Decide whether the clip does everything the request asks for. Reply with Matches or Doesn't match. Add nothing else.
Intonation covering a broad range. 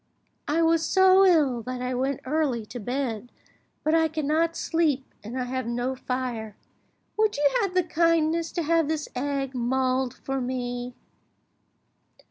Doesn't match